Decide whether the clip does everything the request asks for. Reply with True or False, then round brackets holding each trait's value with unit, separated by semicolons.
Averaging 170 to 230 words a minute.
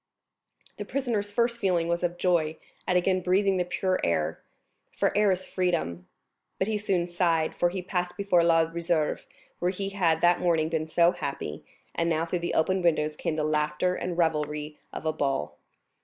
True (180 wpm)